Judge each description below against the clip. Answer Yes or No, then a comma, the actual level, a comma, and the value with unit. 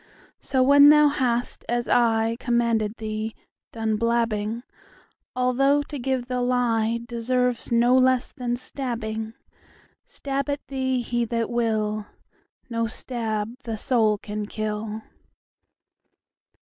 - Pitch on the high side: Yes, high, 235 Hz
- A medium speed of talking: No, slow, 95 wpm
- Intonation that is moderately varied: No, narrow, 2.3 semitones